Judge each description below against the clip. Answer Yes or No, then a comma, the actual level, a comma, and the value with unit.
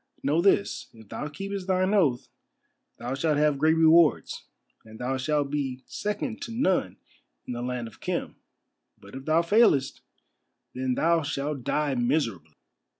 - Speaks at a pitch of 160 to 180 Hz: No, medium, 145 Hz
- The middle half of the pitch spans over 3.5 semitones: Yes, average, 4.9 semitones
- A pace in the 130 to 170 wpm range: Yes, average, 150 wpm